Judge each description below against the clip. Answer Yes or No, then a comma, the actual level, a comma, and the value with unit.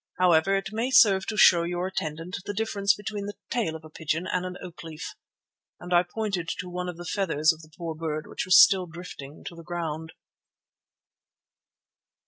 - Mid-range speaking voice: Yes, medium, 175 Hz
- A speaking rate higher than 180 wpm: Yes, average, 190 wpm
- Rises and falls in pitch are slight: No, average, 3.1 semitones